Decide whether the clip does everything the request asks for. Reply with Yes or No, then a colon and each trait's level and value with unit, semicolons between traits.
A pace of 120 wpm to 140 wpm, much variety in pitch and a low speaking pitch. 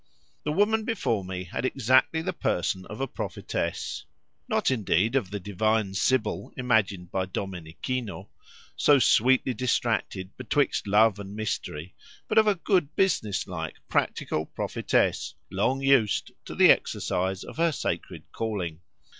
Yes: slow, 135 wpm; wide, 5.9 semitones; low, 110 Hz